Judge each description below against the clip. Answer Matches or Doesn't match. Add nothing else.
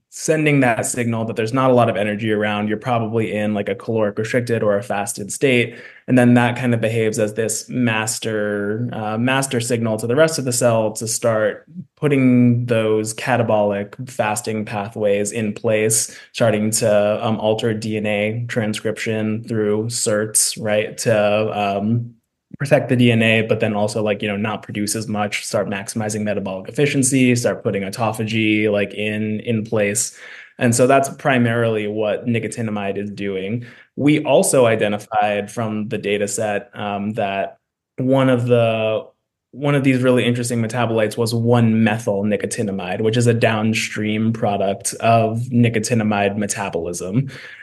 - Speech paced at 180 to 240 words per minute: Doesn't match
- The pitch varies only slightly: Matches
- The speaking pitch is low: Matches